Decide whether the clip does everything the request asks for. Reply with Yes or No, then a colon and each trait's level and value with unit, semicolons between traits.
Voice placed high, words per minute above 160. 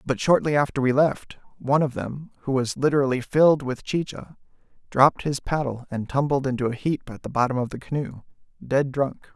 No: low, 135 Hz; average, 190 wpm